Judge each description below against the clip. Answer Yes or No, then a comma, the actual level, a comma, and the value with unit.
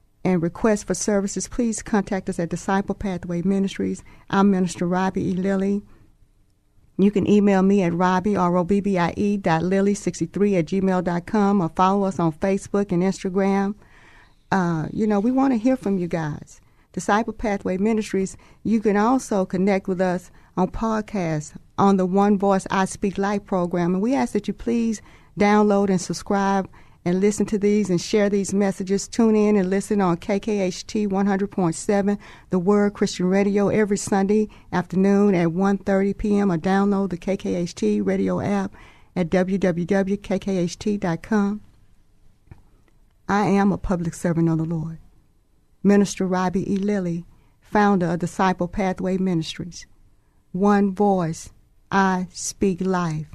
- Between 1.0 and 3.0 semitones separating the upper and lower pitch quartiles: Yes, narrow, 2.5 semitones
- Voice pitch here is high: Yes, high, 195 Hz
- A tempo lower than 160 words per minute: Yes, average, 140 wpm